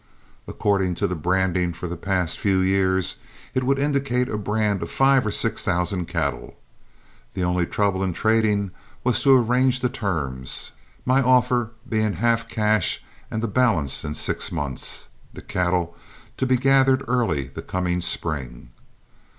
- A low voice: Yes, low, 100 Hz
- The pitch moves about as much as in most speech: No, wide, 5.7 semitones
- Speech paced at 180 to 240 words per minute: No, average, 155 wpm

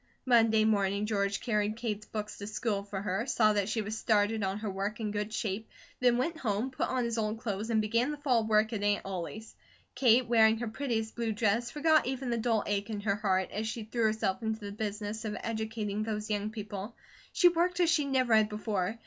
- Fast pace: Yes, fast, 220 wpm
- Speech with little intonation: Yes, narrow, 2.1 semitones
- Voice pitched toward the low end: No, high, 220 Hz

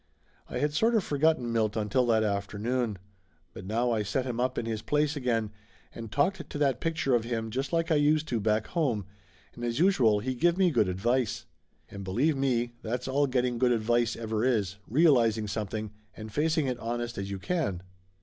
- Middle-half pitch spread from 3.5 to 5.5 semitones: Yes, average, 4.6 semitones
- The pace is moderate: No, fast, 210 wpm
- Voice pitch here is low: Yes, low, 120 Hz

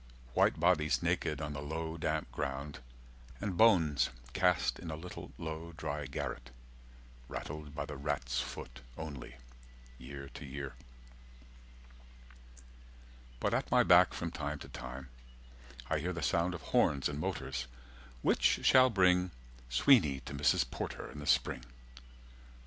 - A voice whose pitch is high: No, very low, 75 Hz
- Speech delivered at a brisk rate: No, average, 140 wpm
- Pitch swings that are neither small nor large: Yes, average, 3.4 semitones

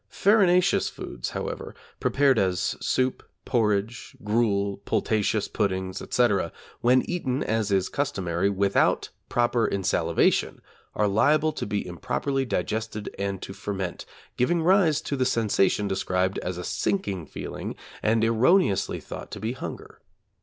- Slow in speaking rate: Yes, slow, 130 wpm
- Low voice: Yes, low, 110 Hz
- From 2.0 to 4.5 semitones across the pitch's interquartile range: No, average, 4.9 semitones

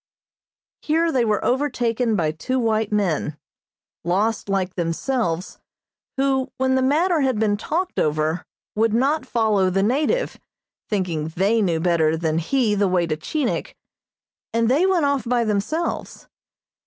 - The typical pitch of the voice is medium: No, high, 220 Hz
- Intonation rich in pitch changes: Yes, wide, 6.5 semitones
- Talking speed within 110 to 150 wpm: Yes, average, 140 wpm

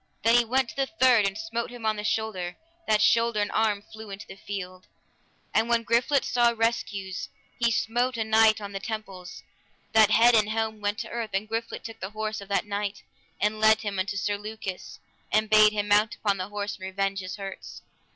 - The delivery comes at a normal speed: No, fast, 215 wpm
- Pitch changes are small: Yes, narrow, 1.9 semitones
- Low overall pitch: No, high, 215 Hz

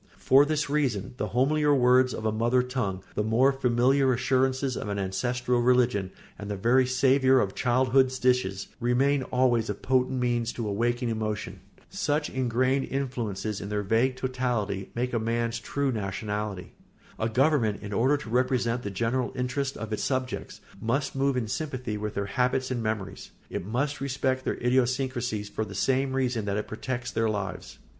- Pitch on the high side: No, low, 125 Hz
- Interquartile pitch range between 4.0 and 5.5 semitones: No, average, 3.2 semitones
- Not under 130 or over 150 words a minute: No, average, 170 wpm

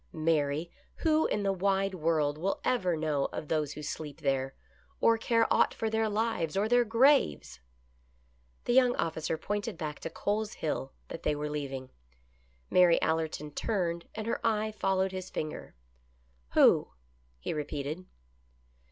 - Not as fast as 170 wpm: Yes, average, 160 wpm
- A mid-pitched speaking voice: Yes, medium, 165 Hz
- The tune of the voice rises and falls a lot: Yes, wide, 6.1 semitones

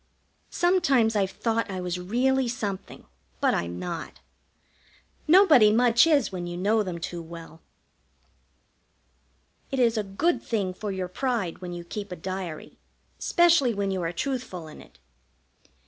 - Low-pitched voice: No, high, 200 Hz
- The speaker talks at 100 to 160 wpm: Yes, average, 145 wpm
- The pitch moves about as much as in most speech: No, wide, 5.7 semitones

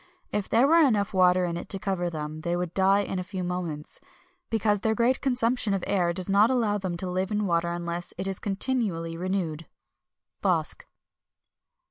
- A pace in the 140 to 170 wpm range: No, average, 185 wpm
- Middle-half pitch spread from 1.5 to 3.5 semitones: Yes, average, 3.1 semitones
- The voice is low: No, high, 190 Hz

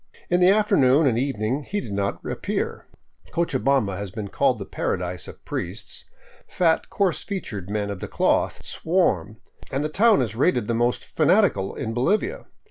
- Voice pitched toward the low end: Yes, low, 130 Hz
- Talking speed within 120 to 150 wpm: No, average, 165 wpm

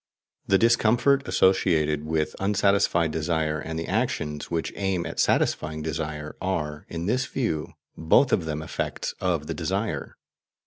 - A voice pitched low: Yes, very low, 80 Hz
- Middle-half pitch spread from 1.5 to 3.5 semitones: No, average, 4.0 semitones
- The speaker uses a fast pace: No, average, 140 wpm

